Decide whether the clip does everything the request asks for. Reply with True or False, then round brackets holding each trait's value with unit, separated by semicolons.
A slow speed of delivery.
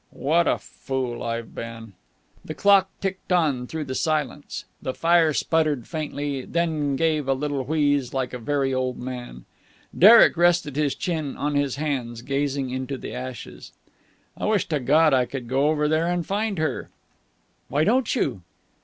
False (165 wpm)